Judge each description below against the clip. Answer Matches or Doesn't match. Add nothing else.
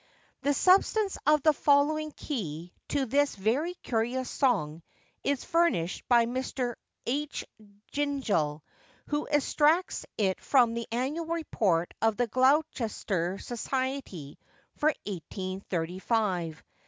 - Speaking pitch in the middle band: Doesn't match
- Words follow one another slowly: Matches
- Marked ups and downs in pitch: Matches